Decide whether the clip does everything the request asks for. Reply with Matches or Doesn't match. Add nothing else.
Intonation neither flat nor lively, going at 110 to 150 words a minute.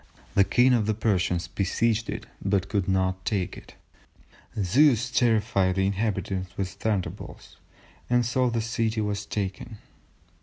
Matches